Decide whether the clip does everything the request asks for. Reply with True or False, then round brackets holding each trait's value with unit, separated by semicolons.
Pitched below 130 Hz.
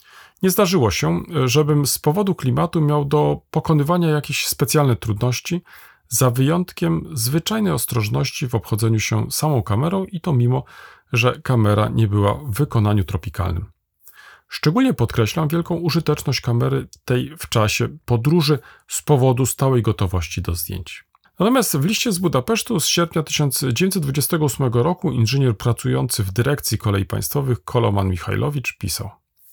False (135 Hz)